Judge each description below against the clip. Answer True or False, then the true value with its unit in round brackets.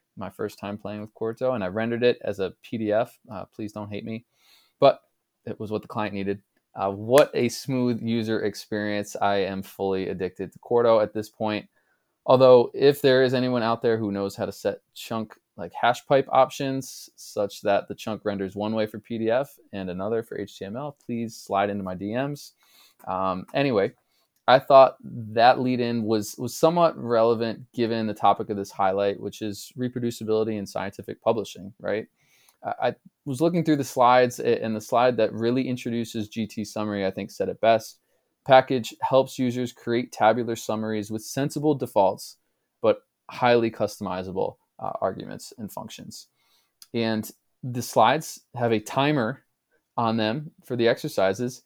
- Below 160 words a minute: False (170 wpm)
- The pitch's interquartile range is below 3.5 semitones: True (3.1 semitones)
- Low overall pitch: True (115 Hz)